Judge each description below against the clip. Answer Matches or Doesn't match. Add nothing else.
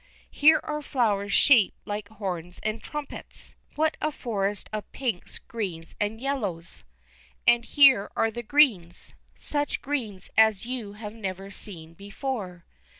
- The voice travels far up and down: Doesn't match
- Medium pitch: Doesn't match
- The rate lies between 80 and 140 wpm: Matches